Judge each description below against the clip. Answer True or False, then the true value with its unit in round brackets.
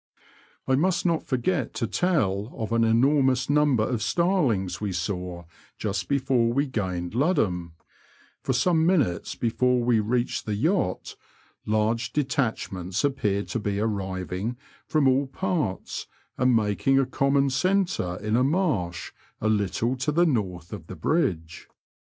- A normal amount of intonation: False (5.8 semitones)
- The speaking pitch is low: True (120 Hz)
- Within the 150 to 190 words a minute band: False (140 wpm)